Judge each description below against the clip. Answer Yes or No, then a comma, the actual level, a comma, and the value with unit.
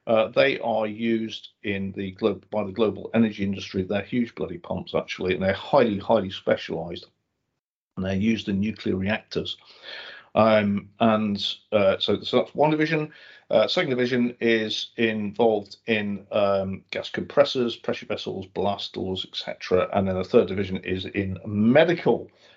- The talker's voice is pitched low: Yes, low, 105 Hz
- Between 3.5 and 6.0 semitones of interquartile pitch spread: No, average, 2.8 semitones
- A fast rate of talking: No, average, 155 wpm